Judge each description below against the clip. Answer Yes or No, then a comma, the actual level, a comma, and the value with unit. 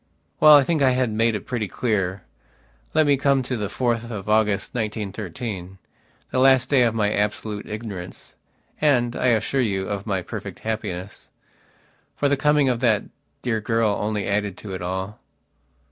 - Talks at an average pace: Yes, average, 165 wpm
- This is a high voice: No, low, 110 Hz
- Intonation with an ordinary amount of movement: Yes, average, 3.7 semitones